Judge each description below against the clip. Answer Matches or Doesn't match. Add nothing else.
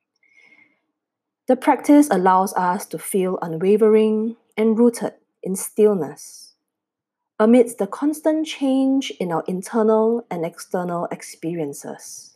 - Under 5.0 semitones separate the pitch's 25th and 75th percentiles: Matches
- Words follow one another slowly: Matches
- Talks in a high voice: Matches